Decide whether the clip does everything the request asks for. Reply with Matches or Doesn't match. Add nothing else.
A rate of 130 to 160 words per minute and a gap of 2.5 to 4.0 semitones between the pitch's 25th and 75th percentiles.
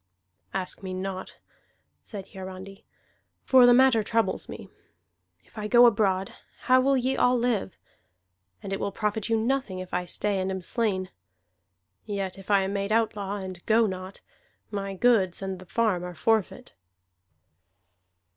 Matches